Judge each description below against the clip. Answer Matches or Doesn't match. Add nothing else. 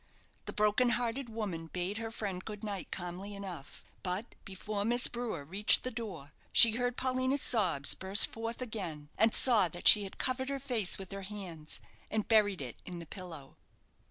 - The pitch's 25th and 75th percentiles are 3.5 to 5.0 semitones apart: Matches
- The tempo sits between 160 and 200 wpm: Matches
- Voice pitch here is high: Matches